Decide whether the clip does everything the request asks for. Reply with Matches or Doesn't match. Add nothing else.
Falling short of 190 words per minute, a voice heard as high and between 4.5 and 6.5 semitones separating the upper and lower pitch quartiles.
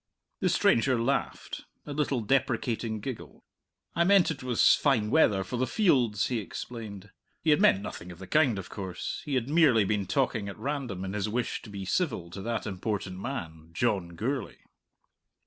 Doesn't match